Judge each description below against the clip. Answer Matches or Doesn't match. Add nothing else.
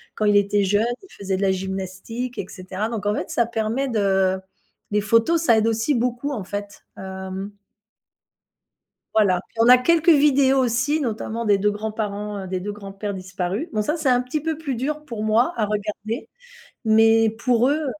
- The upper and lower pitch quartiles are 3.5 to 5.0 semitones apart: Matches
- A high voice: Matches